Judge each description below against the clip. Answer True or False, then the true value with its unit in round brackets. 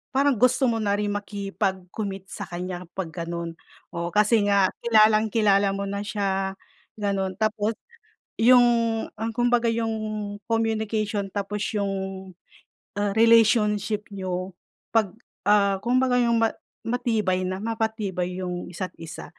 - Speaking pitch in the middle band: False (205 Hz)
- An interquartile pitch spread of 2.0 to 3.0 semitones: True (2.7 semitones)